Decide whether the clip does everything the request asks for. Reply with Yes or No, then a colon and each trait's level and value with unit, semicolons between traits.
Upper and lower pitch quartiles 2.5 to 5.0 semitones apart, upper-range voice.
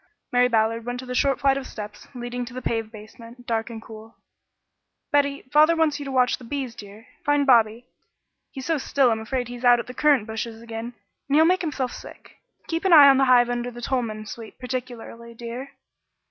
Yes: average, 2.9 semitones; high, 245 Hz